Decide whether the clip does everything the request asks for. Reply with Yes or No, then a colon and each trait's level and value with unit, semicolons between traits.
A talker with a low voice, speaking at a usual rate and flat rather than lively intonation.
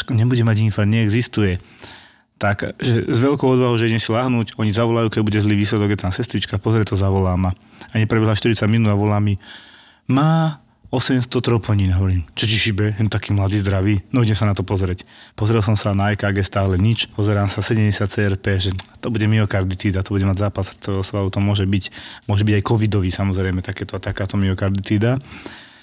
No: low, 105 Hz; fast, 190 wpm; narrow, 2.3 semitones